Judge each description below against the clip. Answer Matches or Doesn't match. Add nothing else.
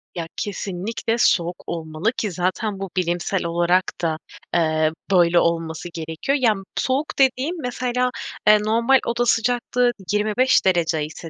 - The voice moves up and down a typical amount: Doesn't match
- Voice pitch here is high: Matches